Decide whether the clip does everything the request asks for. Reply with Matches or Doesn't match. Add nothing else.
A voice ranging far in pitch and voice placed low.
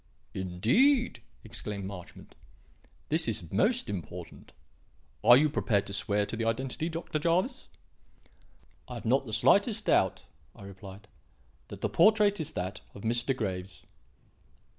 Matches